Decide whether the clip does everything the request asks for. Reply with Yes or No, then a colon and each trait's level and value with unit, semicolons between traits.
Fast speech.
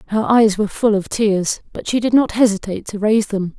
Yes: fast, 235 wpm